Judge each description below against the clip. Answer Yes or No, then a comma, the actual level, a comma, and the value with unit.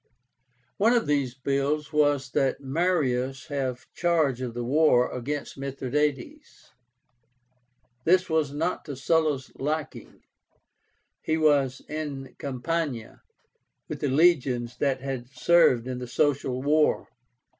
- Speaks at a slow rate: Yes, slow, 115 wpm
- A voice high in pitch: No, medium, 140 Hz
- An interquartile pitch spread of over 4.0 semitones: No, average, 3.1 semitones